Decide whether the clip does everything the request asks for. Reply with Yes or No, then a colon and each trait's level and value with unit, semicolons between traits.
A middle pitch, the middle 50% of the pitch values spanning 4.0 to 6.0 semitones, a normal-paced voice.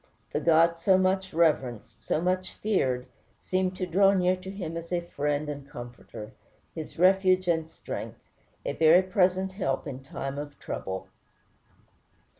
Yes: medium, 170 Hz; average, 4.4 semitones; average, 150 wpm